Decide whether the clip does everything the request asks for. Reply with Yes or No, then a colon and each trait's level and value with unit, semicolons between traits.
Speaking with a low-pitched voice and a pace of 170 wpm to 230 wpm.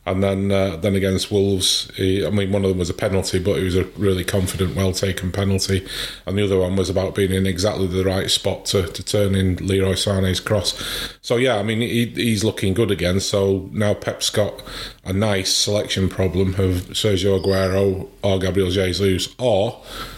Yes: very low, 95 Hz; average, 200 wpm